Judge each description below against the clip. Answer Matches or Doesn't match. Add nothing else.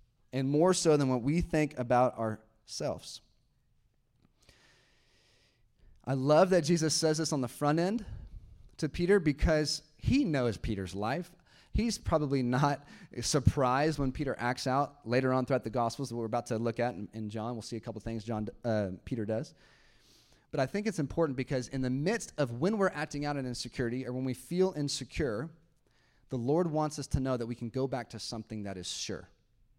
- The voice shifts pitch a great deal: Doesn't match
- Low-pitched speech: Matches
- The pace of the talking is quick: Doesn't match